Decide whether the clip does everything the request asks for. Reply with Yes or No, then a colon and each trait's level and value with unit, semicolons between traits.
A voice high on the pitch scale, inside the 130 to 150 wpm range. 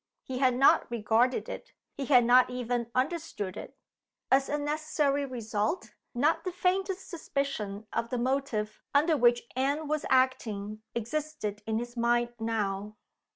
Yes: very high, 250 Hz; average, 145 wpm